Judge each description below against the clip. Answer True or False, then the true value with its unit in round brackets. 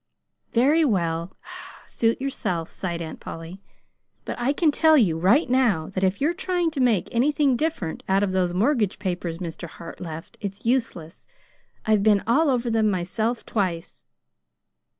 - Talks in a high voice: True (210 Hz)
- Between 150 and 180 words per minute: True (155 wpm)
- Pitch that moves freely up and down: True (6.8 semitones)